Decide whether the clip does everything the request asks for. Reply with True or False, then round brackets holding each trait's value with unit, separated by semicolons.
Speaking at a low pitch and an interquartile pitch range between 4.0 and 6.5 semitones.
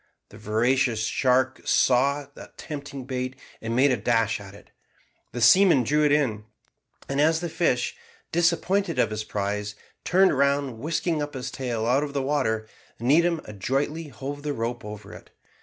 True (130 Hz; 4.6 semitones)